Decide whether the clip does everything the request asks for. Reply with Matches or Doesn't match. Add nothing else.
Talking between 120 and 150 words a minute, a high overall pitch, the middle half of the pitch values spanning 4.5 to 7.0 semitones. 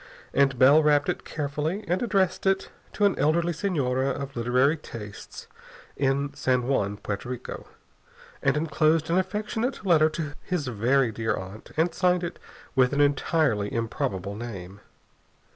Doesn't match